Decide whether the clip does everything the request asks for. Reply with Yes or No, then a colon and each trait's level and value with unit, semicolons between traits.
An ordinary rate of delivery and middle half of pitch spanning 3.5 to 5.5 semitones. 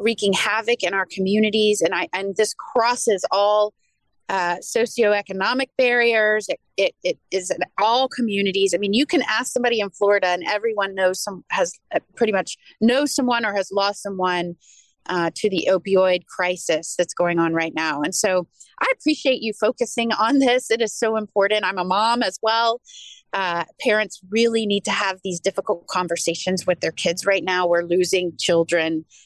Yes: average, 180 wpm; average, 4.0 semitones